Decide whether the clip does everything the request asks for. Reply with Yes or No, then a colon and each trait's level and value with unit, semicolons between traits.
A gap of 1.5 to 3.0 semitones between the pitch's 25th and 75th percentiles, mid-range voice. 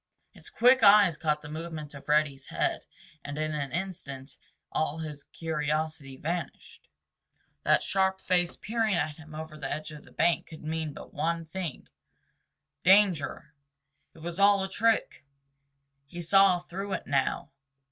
No: average, 3.9 semitones; medium, 160 Hz